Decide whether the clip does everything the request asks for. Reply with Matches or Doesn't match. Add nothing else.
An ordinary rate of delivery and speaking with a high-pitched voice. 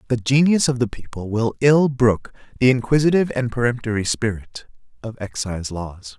Doesn't match